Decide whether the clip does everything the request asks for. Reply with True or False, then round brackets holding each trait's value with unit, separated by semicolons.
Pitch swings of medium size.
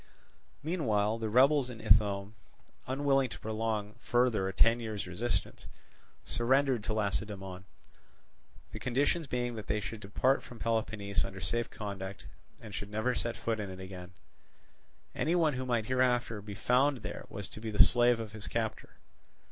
True (3.4 semitones)